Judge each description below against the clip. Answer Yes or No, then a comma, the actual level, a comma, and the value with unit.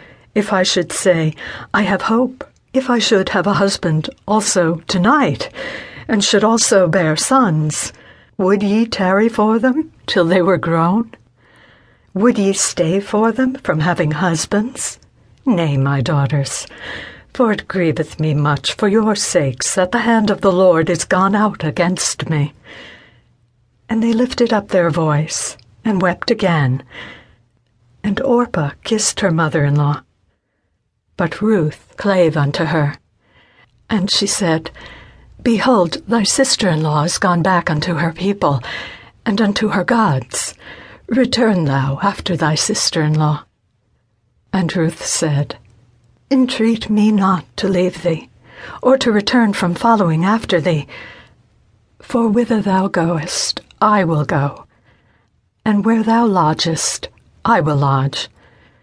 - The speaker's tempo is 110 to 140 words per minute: Yes, slow, 135 wpm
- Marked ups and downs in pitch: Yes, wide, 6.0 semitones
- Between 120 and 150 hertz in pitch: No, medium, 185 Hz